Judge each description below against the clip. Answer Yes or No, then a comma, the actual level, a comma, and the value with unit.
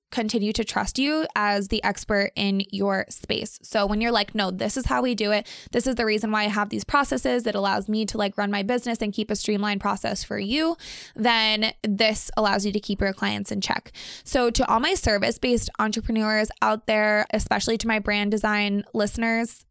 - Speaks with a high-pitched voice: Yes, high, 215 Hz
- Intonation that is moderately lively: No, narrow, 1.8 semitones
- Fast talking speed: Yes, fast, 215 wpm